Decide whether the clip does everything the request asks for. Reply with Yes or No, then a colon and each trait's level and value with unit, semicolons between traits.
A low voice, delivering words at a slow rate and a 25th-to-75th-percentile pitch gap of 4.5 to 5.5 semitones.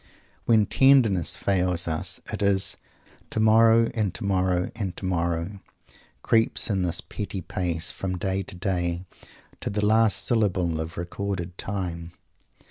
No: very low, 95 Hz; slow, 130 wpm; average, 3.0 semitones